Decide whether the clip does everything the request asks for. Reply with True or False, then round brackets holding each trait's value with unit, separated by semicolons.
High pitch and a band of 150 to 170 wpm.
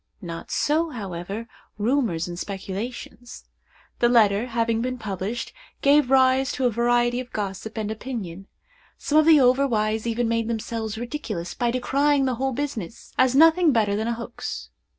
True (235 Hz; 160 wpm)